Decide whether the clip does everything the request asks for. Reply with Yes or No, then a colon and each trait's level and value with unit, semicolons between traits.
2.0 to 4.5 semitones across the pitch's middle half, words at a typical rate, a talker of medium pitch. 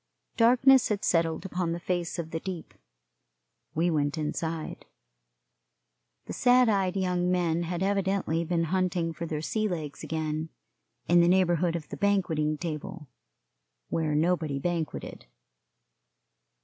No: narrow, 2.6 semitones; slow, 130 wpm; medium, 170 Hz